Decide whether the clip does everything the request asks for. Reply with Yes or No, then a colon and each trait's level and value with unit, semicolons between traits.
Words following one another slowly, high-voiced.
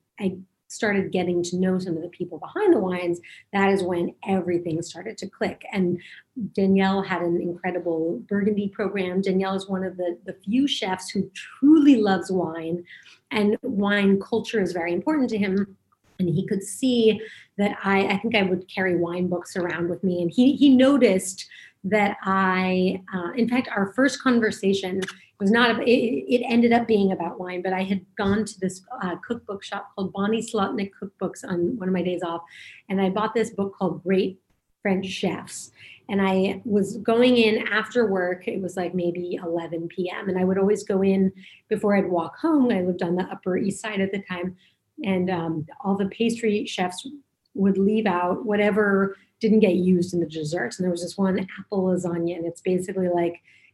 No: average, 190 wpm; high, 195 Hz